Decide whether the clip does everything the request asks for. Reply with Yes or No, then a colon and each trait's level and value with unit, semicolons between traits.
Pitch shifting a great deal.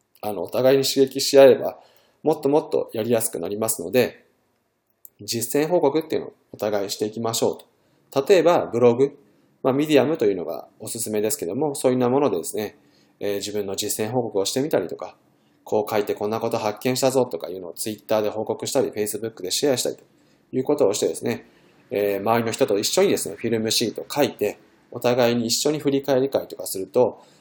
No: average, 3.9 semitones